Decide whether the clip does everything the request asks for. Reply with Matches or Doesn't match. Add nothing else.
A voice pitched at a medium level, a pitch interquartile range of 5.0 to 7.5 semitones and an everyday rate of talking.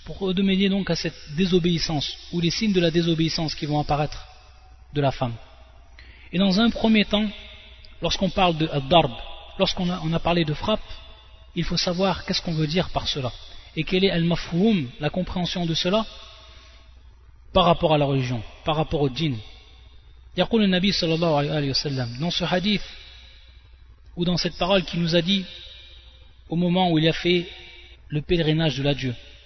Matches